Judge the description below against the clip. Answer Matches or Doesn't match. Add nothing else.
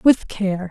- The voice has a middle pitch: Doesn't match